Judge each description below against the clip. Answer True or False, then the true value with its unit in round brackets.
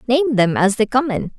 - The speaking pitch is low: False (240 Hz)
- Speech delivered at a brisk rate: True (260 wpm)